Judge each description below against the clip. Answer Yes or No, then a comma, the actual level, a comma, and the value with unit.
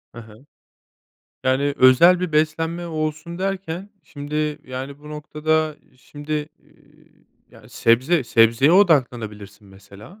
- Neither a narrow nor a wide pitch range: Yes, average, 4.1 semitones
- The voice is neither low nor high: Yes, medium, 150 Hz